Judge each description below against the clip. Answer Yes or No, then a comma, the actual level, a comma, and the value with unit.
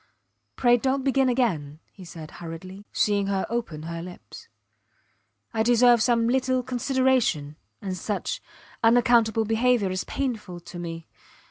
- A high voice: Yes, high, 220 Hz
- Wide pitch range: Yes, wide, 5.7 semitones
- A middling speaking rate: No, slow, 130 wpm